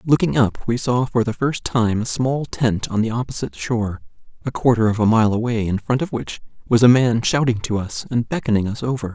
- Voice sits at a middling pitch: No, low, 115 Hz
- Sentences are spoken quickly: Yes, fast, 230 wpm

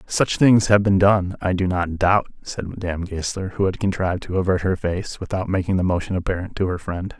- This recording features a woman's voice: No, male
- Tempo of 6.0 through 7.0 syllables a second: No, 5.6 syllables/s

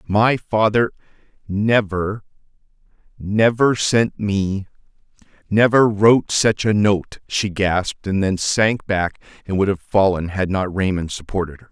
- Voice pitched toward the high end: No, low, 100 Hz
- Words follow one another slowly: Yes, slow, 120 wpm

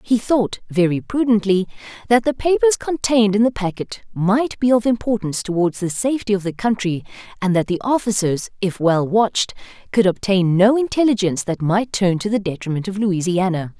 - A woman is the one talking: Yes, female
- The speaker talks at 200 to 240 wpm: No, average, 175 wpm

